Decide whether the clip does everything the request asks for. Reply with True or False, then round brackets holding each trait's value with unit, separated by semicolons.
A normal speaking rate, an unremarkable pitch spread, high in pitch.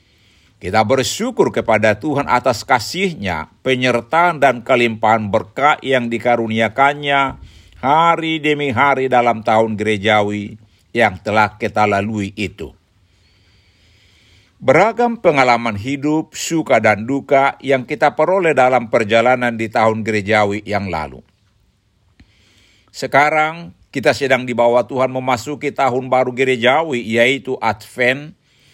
False (105 wpm; 4.6 semitones; 120 Hz)